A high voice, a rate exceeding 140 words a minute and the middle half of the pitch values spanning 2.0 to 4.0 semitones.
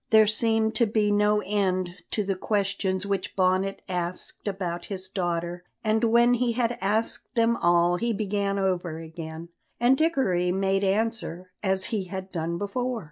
Yes: high, 195 Hz; average, 160 wpm; average, 3.3 semitones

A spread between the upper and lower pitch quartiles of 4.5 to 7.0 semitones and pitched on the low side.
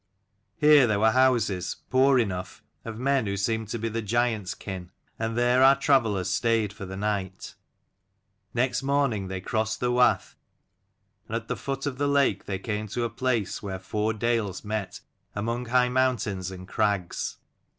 No: average, 3.8 semitones; low, 110 Hz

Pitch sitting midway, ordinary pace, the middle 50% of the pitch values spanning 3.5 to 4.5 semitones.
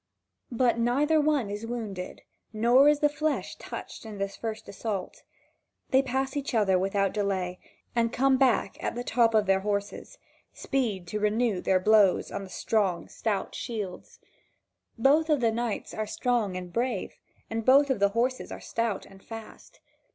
No: high, 225 Hz; average, 165 wpm; average, 4.2 semitones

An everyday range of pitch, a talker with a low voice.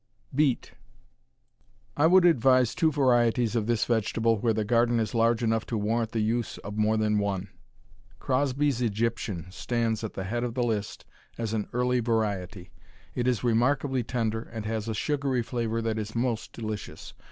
No: narrow, 2.2 semitones; low, 115 Hz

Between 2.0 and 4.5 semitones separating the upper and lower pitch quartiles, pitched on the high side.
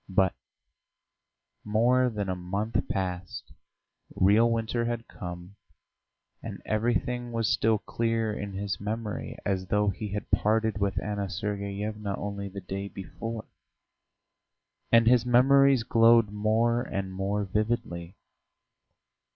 No: average, 2.7 semitones; low, 105 Hz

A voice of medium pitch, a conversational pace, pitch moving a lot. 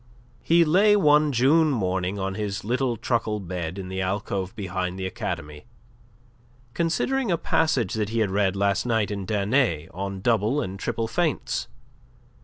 No: low, 105 Hz; average, 155 wpm; wide, 6.0 semitones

